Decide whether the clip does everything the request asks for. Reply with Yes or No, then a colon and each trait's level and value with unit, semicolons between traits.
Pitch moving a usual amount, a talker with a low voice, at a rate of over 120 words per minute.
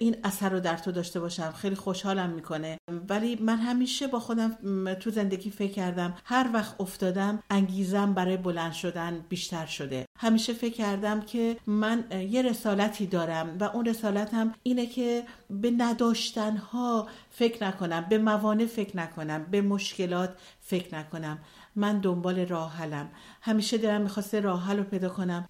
No: average, 3.9 semitones; high, 200 Hz; average, 150 wpm